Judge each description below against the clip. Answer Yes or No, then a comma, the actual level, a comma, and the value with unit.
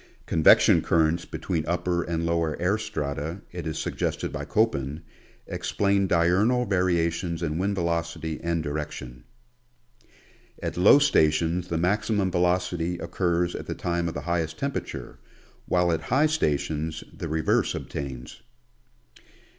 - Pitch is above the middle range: No, very low, 85 Hz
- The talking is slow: Yes, slow, 130 wpm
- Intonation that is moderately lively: No, narrow, 2.2 semitones